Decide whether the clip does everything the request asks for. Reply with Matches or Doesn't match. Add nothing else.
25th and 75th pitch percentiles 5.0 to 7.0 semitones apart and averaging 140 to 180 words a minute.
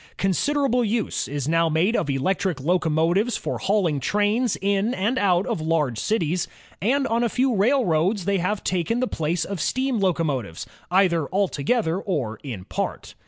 Matches